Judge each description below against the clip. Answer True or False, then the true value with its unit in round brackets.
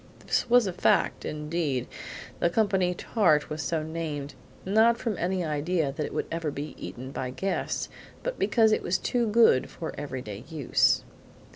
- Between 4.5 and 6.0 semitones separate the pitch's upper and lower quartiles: True (5.1 semitones)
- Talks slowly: False (170 wpm)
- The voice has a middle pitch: True (165 Hz)